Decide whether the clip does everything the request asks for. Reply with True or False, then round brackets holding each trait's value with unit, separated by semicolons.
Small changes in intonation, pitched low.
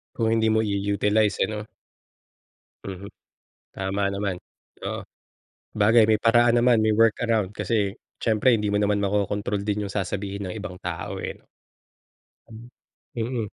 True (1.9 semitones; 105 Hz)